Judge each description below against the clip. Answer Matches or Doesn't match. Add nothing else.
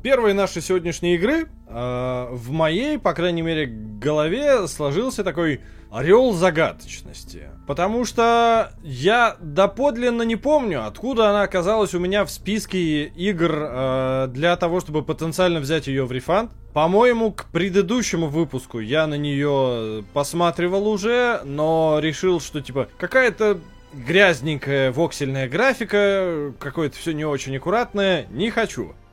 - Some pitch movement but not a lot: Doesn't match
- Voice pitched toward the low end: Doesn't match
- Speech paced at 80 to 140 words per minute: Matches